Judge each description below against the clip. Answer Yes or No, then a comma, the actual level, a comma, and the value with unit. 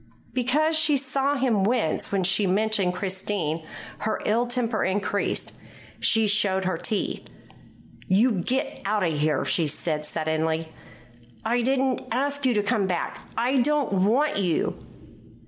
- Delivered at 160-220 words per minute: No, average, 140 wpm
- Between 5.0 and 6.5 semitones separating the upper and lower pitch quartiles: Yes, wide, 5.4 semitones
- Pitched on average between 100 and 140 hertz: No, high, 210 Hz